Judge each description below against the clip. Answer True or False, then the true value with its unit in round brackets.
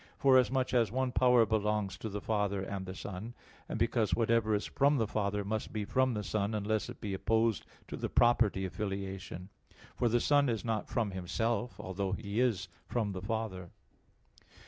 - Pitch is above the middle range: False (110 Hz)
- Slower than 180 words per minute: False (185 wpm)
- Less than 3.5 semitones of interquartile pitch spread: True (3.0 semitones)